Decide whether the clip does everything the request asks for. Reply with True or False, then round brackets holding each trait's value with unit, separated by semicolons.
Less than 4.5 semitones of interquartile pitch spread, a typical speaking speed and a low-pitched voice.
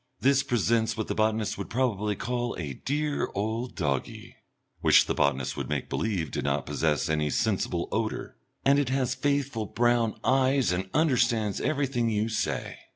False (4.9 semitones; 160 wpm; 110 Hz)